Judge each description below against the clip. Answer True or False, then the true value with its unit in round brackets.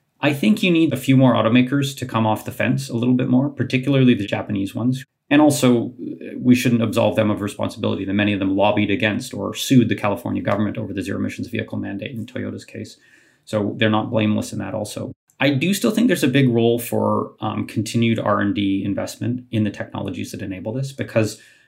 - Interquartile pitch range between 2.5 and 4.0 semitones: True (3.3 semitones)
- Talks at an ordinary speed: False (210 wpm)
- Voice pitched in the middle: False (110 Hz)